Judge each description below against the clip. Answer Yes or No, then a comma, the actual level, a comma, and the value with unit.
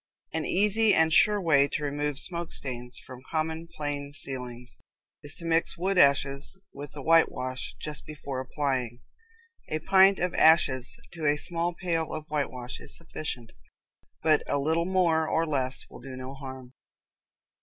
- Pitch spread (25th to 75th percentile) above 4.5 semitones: No, average, 3.9 semitones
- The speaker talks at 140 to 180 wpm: Yes, average, 155 wpm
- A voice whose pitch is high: No, medium, 150 Hz